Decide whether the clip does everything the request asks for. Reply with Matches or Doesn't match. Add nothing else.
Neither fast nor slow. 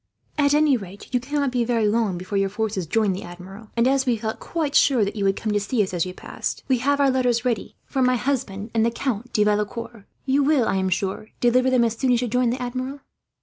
Doesn't match